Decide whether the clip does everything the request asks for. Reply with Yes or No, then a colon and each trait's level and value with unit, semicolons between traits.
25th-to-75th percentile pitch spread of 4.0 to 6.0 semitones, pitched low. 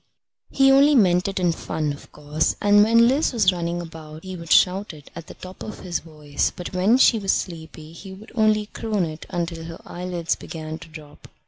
No: average, 4.3 semitones; medium, 175 Hz